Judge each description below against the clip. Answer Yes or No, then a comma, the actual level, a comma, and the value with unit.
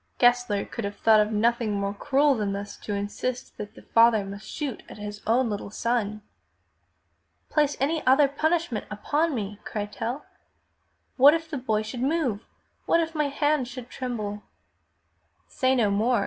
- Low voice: No, high, 235 Hz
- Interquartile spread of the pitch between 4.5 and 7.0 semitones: Yes, average, 4.9 semitones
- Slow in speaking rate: No, average, 165 wpm